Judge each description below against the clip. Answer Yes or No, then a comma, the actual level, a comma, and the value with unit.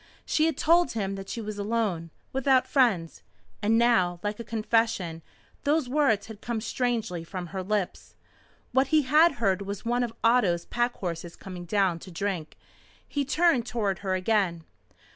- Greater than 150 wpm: Yes, average, 165 wpm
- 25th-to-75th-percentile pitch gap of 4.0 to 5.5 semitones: Yes, average, 4.6 semitones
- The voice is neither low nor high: No, high, 215 Hz